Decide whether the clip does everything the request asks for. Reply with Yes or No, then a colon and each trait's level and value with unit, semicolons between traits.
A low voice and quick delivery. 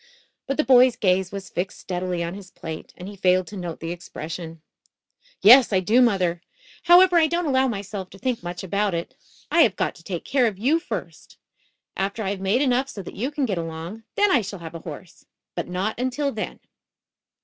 No: high, 195 Hz; fast, 210 wpm